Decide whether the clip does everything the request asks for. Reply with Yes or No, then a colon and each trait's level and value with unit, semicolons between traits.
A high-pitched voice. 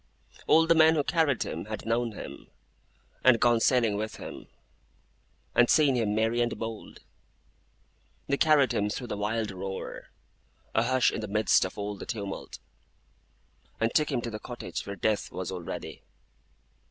No: low, 115 Hz